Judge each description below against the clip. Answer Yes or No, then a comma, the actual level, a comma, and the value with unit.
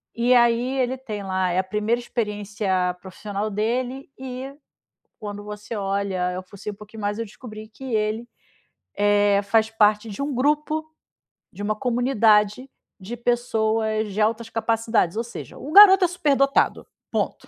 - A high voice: Yes, high, 220 Hz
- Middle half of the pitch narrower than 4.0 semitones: Yes, average, 3.2 semitones